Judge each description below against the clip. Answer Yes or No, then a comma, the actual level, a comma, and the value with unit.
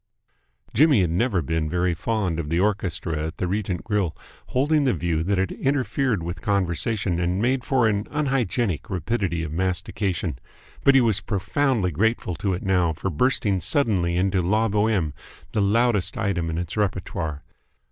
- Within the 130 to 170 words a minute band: Yes, average, 165 wpm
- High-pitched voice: No, very low, 95 Hz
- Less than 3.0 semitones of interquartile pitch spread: No, average, 4.6 semitones